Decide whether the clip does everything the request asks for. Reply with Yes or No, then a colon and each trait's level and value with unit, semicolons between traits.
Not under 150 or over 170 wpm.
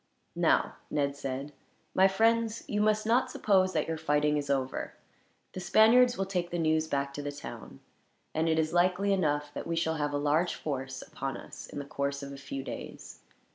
No: average, 200 wpm